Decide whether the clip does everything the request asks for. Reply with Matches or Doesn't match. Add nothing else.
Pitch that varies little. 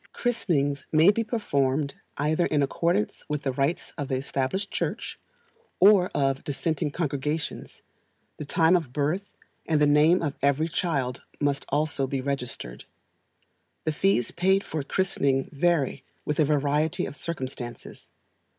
Doesn't match